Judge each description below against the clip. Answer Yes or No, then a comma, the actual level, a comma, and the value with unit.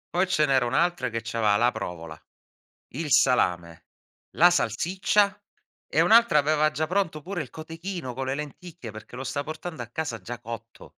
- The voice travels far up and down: Yes, wide, 6.5 semitones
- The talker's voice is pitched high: No, medium, 145 Hz